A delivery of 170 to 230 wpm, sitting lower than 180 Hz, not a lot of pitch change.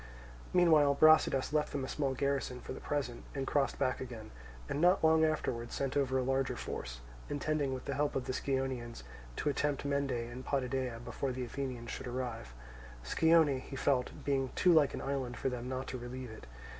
Yes: average, 195 wpm; low, 135 Hz; narrow, 2.2 semitones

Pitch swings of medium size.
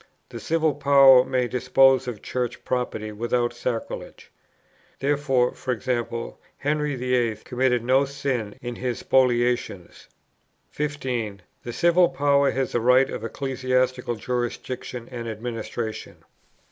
No: narrow, 2.0 semitones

